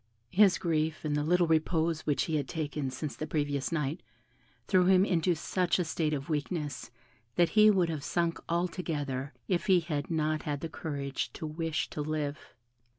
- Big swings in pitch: No, average, 2.7 semitones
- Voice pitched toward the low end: No, medium, 160 Hz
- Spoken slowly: No, average, 180 wpm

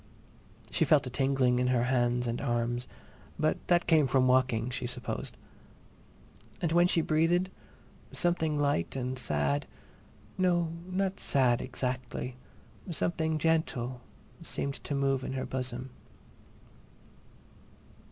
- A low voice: Yes, low, 130 Hz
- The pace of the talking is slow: Yes, slow, 115 wpm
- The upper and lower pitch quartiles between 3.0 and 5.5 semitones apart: Yes, average, 4.4 semitones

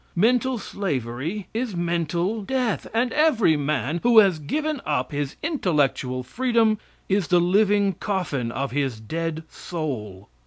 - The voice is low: No, medium, 175 Hz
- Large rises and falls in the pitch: Yes, wide, 7.4 semitones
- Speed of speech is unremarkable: No, slow, 130 wpm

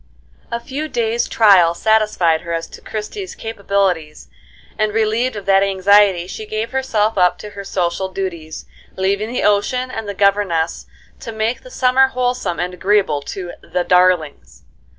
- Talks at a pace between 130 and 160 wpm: Yes, average, 155 wpm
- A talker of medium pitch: No, high, 205 Hz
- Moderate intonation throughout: Yes, average, 3.7 semitones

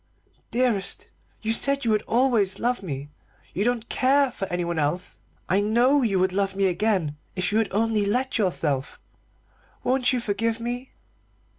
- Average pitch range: Yes, average, 4.5 semitones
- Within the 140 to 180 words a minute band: Yes, average, 160 wpm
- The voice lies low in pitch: No, high, 215 Hz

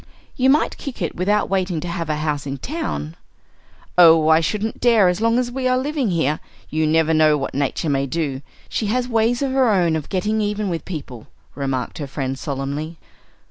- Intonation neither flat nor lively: No, wide, 6.9 semitones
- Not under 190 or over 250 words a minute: Yes, average, 200 wpm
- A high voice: No, medium, 170 Hz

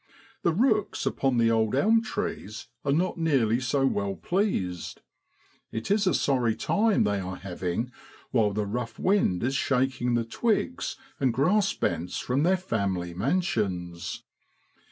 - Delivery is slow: No, average, 145 wpm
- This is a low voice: Yes, low, 125 Hz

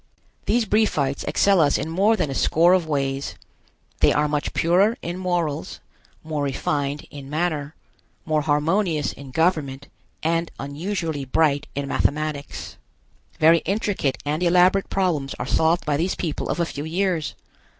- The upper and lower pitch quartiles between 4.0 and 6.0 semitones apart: No, average, 3.6 semitones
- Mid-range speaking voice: Yes, medium, 155 Hz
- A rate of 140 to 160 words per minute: Yes, average, 150 wpm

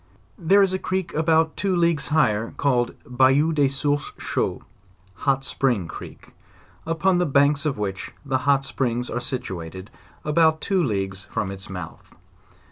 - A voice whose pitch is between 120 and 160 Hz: Yes, medium, 140 Hz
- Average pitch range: No, wide, 5.7 semitones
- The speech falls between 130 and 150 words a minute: No, average, 160 wpm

